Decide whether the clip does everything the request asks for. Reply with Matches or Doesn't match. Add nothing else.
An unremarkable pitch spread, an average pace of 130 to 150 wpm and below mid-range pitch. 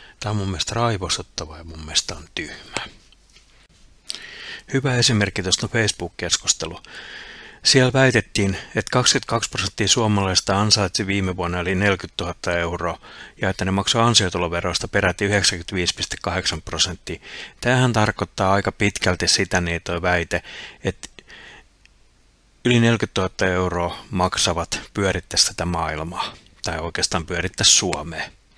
Doesn't match